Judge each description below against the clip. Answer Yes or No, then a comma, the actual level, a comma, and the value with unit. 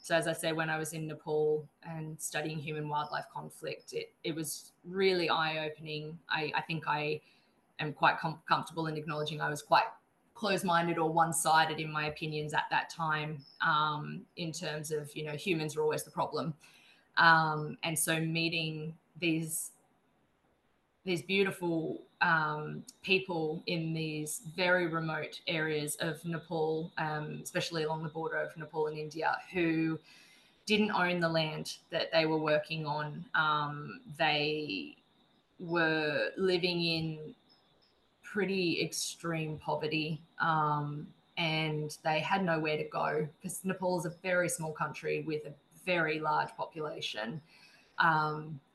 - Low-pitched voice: No, medium, 160 Hz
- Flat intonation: Yes, narrow, 1.7 semitones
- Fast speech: No, average, 145 wpm